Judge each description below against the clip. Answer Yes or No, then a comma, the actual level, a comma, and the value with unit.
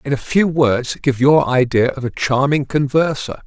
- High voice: No, low, 135 Hz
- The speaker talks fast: No, average, 190 wpm